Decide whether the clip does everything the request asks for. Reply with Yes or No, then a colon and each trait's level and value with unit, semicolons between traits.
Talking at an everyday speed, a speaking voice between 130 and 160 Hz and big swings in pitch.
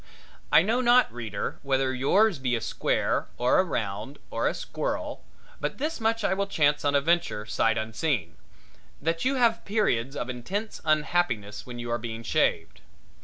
Yes: average, 175 wpm; medium, 140 Hz; wide, 8.7 semitones